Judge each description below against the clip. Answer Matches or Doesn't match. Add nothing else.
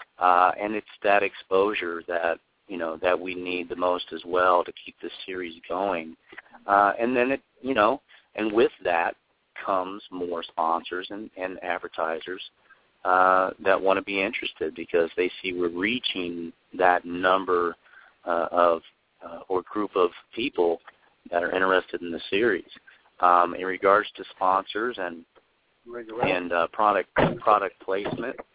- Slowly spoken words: Doesn't match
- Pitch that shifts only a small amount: Matches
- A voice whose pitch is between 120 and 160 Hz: Doesn't match